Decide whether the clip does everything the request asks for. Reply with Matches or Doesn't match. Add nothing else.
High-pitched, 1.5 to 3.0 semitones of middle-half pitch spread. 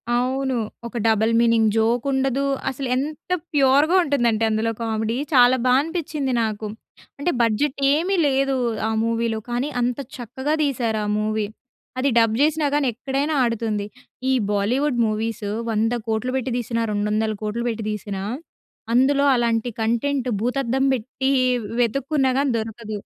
Doesn't match